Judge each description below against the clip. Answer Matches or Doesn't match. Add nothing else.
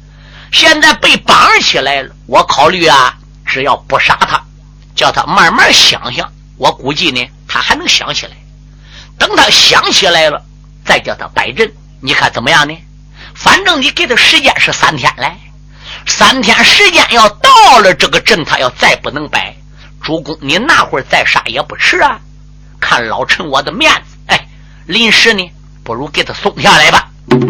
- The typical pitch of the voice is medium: Matches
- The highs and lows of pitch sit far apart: Matches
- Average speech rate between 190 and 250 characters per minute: Matches